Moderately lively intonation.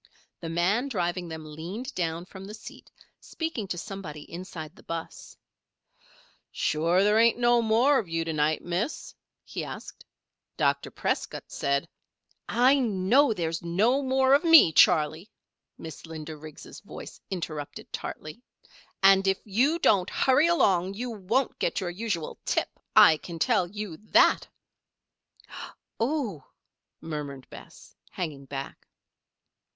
No: wide, 6.1 semitones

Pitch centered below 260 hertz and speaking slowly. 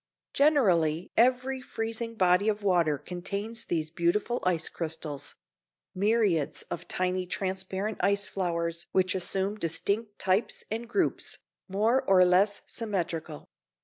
Yes: high, 190 Hz; slow, 115 wpm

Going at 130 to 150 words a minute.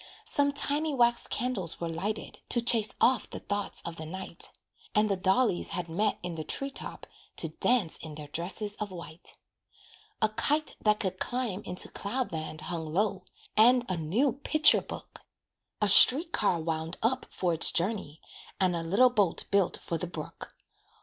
No: average, 175 wpm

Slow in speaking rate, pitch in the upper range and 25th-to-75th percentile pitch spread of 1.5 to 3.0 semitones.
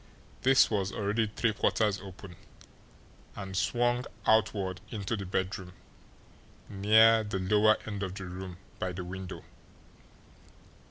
No: slow, 120 wpm; low, 100 Hz; narrow, 2.6 semitones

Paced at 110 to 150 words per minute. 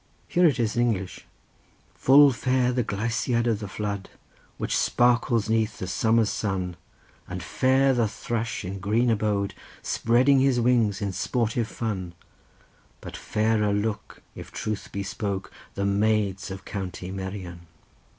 Yes: average, 140 wpm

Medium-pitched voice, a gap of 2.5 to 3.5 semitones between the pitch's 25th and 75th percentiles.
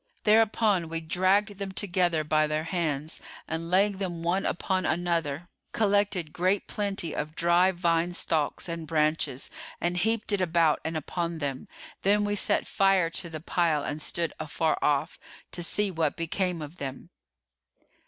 Yes: medium, 170 Hz; average, 3.2 semitones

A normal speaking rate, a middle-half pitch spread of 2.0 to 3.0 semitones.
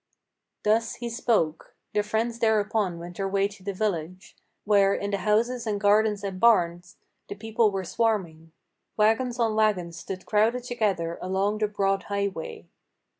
Yes: average, 155 wpm; average, 2.7 semitones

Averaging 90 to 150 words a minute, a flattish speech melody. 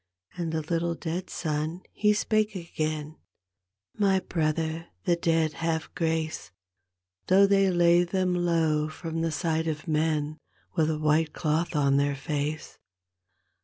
Yes: average, 140 wpm; narrow, 2.0 semitones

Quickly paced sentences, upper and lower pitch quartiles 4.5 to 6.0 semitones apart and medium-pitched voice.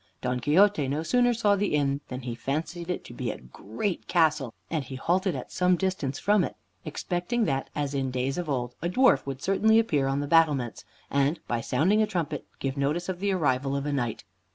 Yes: fast, 215 wpm; average, 5.3 semitones; medium, 150 Hz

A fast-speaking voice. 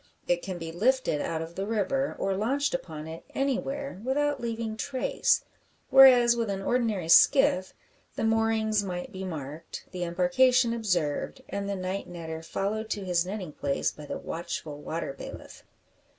No: average, 160 wpm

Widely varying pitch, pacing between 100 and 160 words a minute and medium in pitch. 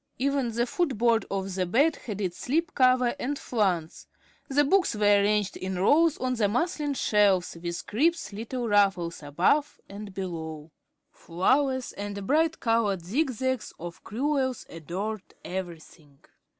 No: wide, 5.9 semitones; average, 145 wpm; high, 215 Hz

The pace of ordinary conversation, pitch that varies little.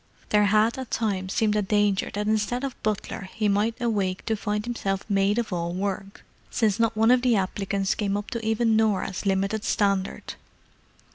Yes: average, 185 wpm; narrow, 2.2 semitones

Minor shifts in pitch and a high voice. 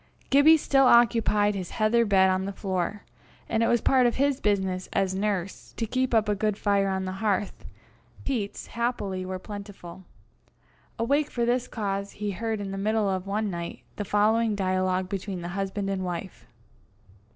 No: average, 3.1 semitones; high, 205 Hz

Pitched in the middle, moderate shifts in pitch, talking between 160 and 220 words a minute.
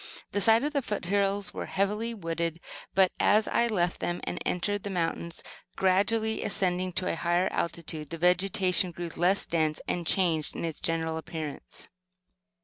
Yes: medium, 180 Hz; average, 3.1 semitones; average, 165 wpm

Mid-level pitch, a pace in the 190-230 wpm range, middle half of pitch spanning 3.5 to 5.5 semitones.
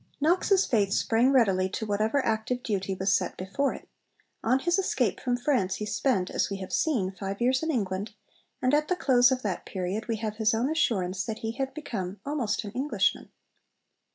No: high, 225 Hz; average, 195 wpm; average, 5.2 semitones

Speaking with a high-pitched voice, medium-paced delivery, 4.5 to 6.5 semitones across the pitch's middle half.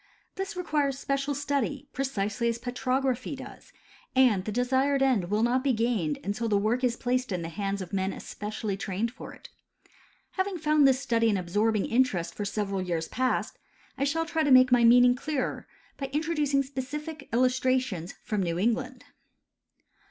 Yes: very high, 250 Hz; average, 165 wpm; average, 4.8 semitones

